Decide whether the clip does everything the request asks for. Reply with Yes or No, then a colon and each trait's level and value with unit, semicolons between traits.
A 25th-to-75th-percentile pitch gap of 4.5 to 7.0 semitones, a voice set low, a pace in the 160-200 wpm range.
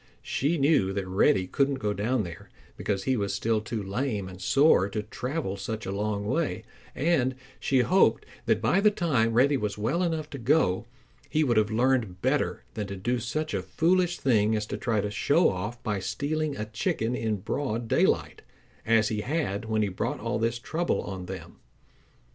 Yes: average, 5.3 semitones; low, 115 Hz; average, 190 wpm